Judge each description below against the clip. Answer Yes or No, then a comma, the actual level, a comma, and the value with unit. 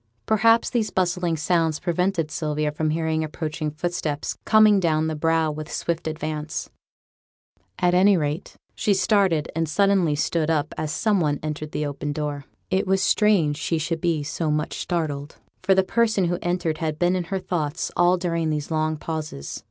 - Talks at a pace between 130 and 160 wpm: No, average, 175 wpm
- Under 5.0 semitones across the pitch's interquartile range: Yes, average, 2.9 semitones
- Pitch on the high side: No, medium, 160 Hz